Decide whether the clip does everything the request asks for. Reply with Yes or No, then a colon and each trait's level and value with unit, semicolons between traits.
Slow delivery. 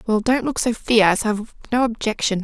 No: average, 200 wpm